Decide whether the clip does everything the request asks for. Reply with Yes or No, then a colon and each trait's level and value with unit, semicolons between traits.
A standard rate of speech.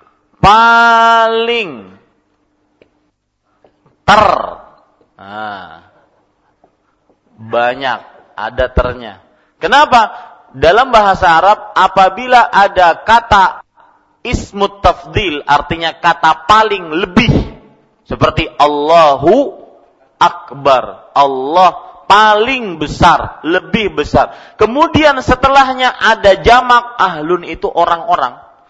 No: slow, 70 wpm